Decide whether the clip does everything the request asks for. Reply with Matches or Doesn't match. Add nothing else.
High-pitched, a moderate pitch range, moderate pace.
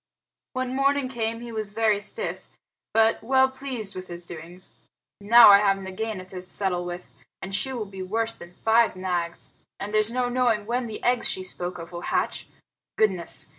Matches